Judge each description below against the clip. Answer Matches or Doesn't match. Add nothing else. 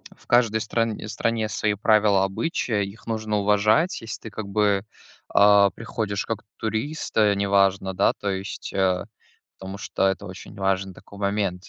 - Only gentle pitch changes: Matches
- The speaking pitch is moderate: Doesn't match